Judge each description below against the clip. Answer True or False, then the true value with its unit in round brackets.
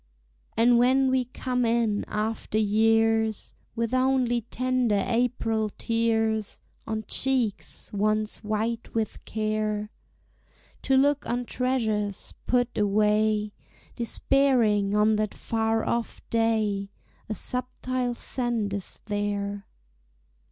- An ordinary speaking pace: False (100 wpm)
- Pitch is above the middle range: True (225 Hz)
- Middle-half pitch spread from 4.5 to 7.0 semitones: False (2.5 semitones)